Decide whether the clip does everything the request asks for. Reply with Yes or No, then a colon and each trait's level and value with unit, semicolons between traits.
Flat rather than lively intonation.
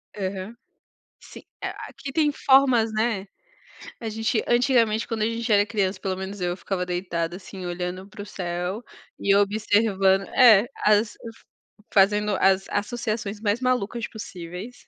No: average, 3.2 semitones